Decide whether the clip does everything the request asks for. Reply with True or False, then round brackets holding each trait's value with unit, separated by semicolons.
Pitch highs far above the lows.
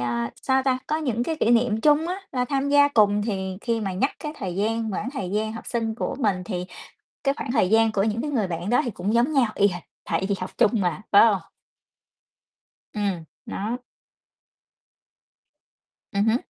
False (4.1 semitones)